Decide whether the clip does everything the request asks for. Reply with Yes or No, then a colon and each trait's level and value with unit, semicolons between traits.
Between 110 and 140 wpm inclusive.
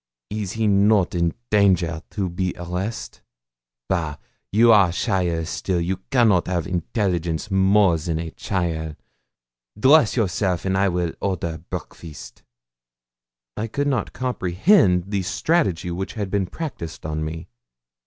Yes: slow, 135 wpm